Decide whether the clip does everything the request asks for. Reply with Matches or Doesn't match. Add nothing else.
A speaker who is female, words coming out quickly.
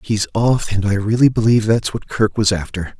Doesn't match